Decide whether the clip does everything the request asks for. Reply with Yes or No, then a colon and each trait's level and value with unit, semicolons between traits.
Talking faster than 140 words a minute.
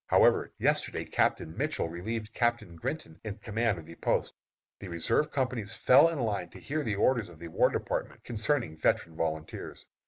Yes: average, 175 wpm